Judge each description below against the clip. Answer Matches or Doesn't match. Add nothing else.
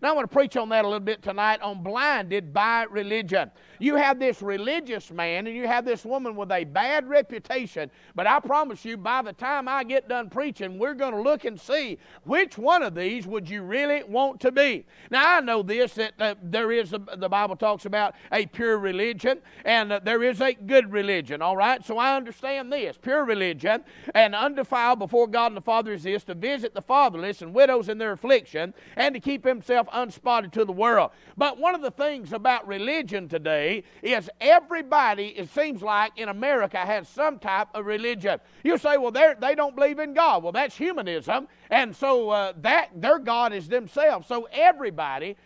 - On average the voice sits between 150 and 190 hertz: Doesn't match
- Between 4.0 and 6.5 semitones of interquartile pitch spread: Matches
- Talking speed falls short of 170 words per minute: Doesn't match